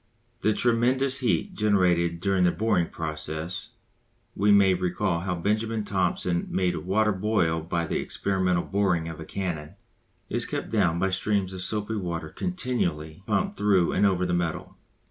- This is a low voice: Yes, very low, 95 Hz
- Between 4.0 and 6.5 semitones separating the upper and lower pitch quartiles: No, average, 3.4 semitones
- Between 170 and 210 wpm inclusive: No, average, 155 wpm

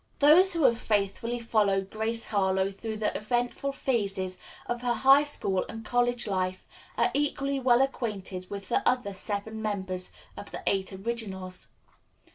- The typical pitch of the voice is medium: No, high, 220 Hz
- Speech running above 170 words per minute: No, average, 150 wpm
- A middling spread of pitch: Yes, average, 3.9 semitones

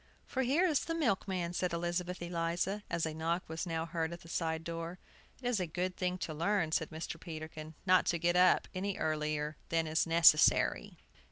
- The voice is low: No, medium, 170 Hz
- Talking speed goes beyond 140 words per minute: Yes, average, 195 wpm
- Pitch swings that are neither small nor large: No, narrow, 2.2 semitones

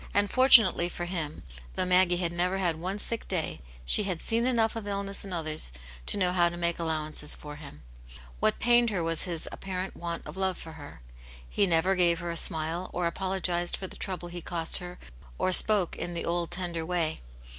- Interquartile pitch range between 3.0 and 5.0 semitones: No, narrow, 2.4 semitones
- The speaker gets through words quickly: Yes, fast, 210 wpm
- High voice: No, medium, 175 Hz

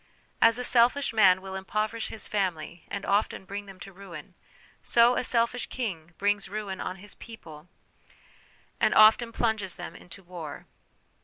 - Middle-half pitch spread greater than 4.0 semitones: No, average, 3.5 semitones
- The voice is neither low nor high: No, high, 200 Hz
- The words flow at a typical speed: Yes, average, 155 wpm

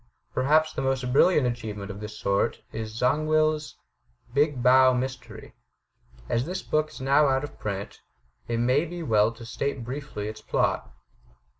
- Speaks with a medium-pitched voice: No, low, 130 Hz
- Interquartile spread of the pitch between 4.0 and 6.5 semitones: Yes, average, 4.6 semitones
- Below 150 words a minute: No, average, 155 wpm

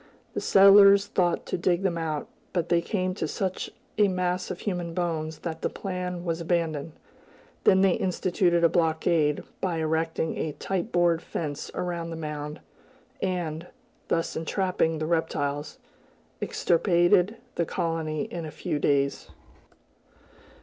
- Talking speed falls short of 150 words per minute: Yes, average, 140 wpm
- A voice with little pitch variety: Yes, narrow, 2.3 semitones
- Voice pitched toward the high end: No, medium, 170 Hz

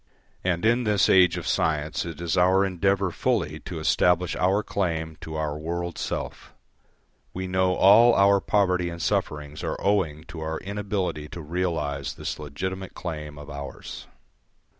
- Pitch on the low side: Yes, very low, 90 Hz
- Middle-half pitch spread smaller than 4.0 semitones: Yes, average, 3.5 semitones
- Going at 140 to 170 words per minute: Yes, average, 155 wpm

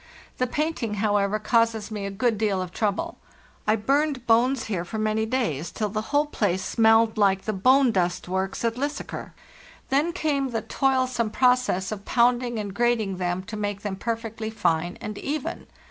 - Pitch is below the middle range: No, high, 220 Hz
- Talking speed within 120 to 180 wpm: Yes, average, 175 wpm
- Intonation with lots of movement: No, average, 3.8 semitones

